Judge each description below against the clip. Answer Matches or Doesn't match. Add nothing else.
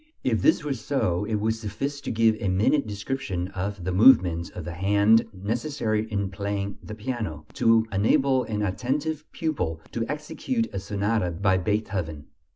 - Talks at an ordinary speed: Matches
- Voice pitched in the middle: Doesn't match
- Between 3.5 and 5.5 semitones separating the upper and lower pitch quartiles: Matches